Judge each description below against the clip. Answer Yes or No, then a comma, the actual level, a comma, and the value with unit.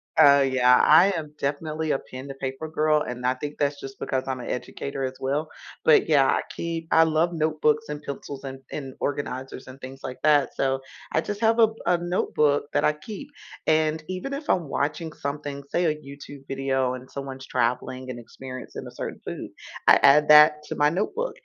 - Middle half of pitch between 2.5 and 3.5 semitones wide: Yes, average, 2.9 semitones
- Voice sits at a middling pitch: Yes, medium, 145 Hz